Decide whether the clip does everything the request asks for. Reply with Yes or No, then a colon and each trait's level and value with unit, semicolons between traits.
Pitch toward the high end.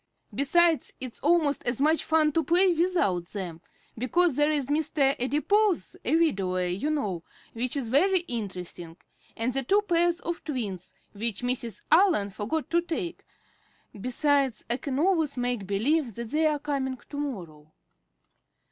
Yes: very high, 275 Hz